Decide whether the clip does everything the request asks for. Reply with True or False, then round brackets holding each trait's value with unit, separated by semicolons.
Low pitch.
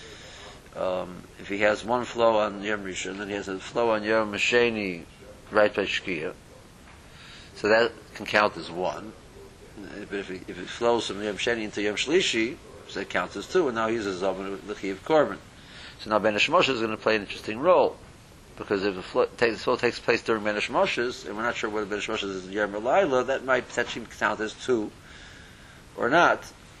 True (105 Hz)